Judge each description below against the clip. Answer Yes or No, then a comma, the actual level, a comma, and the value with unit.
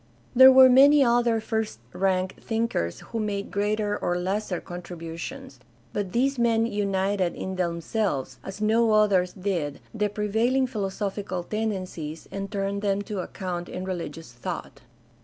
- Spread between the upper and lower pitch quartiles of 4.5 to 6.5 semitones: No, average, 3.5 semitones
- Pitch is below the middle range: No, high, 200 Hz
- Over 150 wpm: No, average, 140 wpm